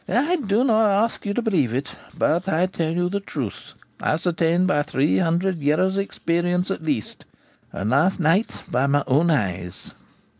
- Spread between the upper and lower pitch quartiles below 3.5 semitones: No, average, 4.9 semitones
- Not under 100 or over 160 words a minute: No, average, 175 wpm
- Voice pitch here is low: No, medium, 170 Hz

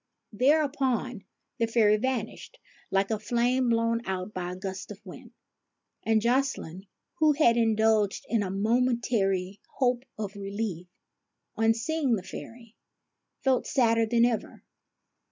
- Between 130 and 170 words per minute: Yes, slow, 135 wpm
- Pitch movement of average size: Yes, average, 3.5 semitones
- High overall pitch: Yes, high, 225 Hz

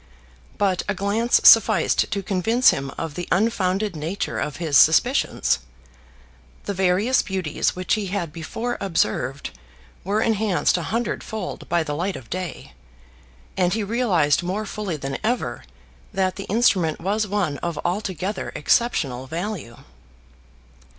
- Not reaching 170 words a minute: Yes, slow, 135 wpm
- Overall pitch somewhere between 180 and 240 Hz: Yes, medium, 185 Hz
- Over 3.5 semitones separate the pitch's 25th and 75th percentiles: Yes, average, 4.4 semitones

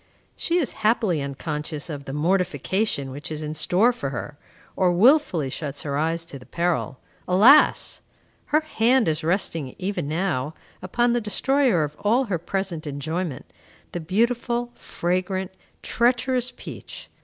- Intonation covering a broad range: Yes, wide, 7.2 semitones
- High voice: No, medium, 180 Hz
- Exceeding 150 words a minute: No, average, 145 wpm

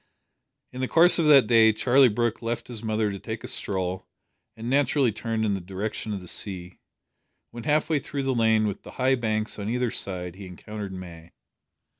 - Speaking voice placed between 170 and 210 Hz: No, low, 110 Hz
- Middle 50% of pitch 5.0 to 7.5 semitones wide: No, average, 4.0 semitones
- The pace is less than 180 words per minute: No, average, 200 wpm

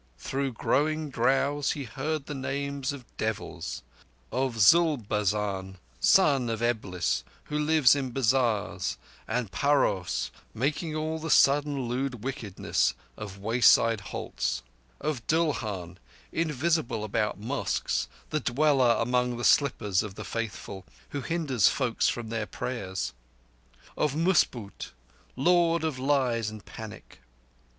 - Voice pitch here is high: No, low, 125 Hz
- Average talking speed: No, slow, 115 wpm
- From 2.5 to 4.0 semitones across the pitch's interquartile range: No, average, 5.3 semitones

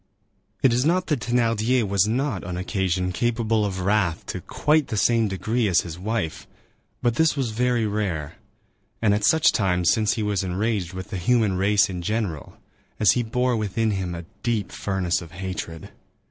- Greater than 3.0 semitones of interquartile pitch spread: Yes, average, 4.1 semitones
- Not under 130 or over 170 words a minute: No, average, 180 wpm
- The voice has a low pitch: Yes, low, 105 Hz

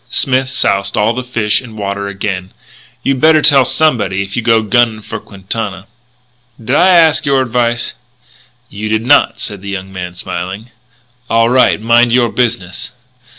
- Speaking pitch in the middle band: No, low, 115 Hz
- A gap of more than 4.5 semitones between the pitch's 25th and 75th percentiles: No, average, 4.0 semitones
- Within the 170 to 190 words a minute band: No, average, 160 wpm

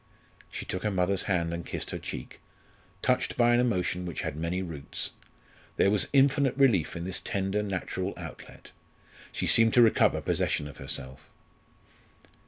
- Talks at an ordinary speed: Yes, average, 160 wpm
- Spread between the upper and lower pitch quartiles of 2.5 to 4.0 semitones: No, average, 5.1 semitones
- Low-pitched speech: Yes, very low, 95 Hz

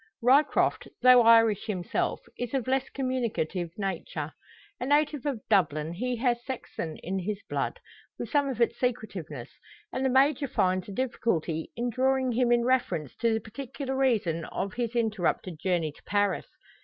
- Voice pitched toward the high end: Yes, high, 230 Hz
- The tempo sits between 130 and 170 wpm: Yes, average, 160 wpm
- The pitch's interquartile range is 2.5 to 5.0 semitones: No, wide, 5.6 semitones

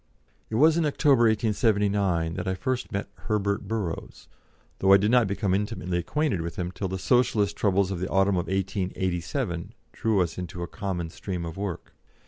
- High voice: No, low, 100 Hz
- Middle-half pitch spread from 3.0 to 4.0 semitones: Yes, average, 3.3 semitones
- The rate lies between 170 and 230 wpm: Yes, average, 180 wpm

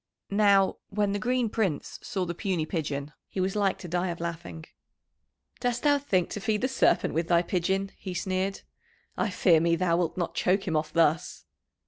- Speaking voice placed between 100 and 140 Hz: No, medium, 185 Hz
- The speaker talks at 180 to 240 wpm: Yes, average, 190 wpm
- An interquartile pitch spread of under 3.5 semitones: Yes, average, 3.0 semitones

